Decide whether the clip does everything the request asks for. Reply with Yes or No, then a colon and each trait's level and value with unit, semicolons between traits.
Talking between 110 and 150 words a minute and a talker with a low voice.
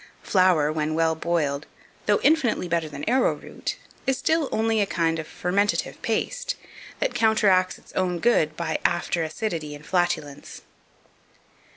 No: average, 140 wpm; medium, 175 Hz